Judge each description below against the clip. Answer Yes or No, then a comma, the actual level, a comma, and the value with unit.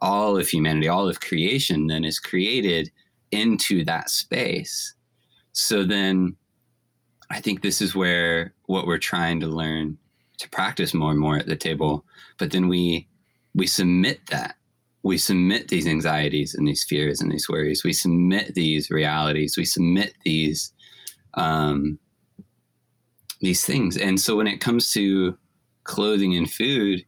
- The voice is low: Yes, very low, 85 Hz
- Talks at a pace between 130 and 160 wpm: Yes, average, 150 wpm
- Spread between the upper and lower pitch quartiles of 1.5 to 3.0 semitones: No, average, 3.6 semitones